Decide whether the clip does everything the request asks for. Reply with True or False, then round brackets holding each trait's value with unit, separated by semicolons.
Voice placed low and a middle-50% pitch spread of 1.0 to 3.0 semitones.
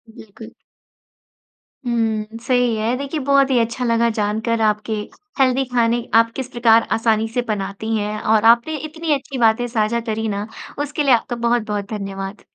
False (230 Hz; 2.4 semitones)